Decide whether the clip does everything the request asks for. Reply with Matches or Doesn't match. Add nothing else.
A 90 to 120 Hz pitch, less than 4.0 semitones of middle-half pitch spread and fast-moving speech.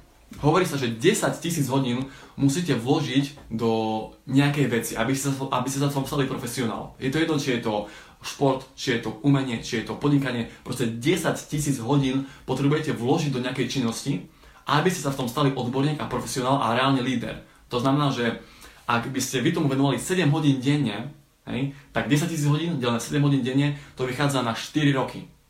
Doesn't match